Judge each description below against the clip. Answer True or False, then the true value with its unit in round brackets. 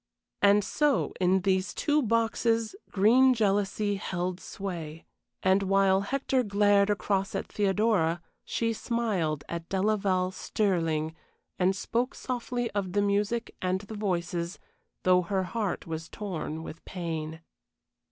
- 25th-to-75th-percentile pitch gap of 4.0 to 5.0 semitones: False (3.1 semitones)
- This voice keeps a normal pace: False (125 wpm)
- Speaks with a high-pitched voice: True (195 Hz)